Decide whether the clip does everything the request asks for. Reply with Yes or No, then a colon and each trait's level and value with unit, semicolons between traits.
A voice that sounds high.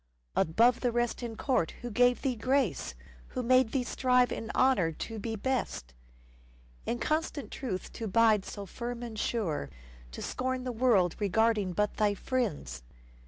Yes: high, 230 Hz